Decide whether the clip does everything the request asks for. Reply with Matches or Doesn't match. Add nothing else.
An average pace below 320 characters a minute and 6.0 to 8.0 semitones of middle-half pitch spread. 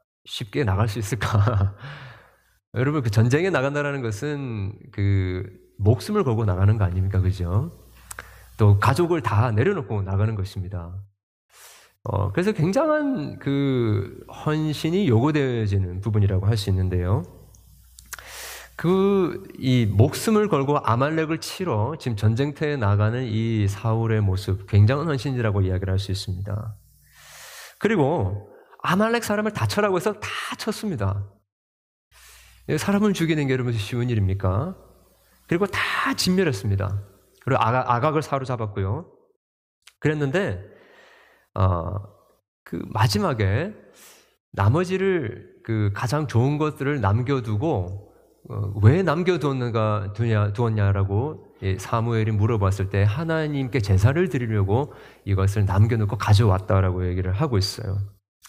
Matches